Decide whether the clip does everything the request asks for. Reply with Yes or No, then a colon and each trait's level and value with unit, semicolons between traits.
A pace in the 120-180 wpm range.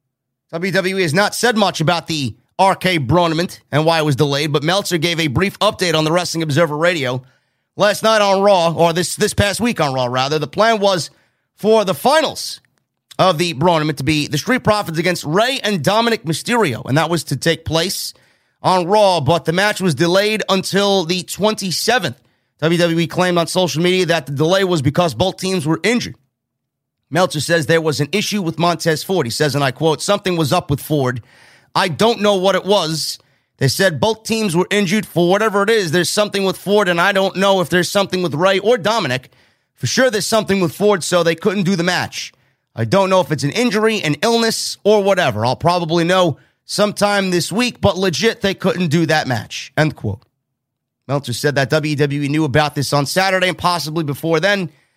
No: fast, 205 wpm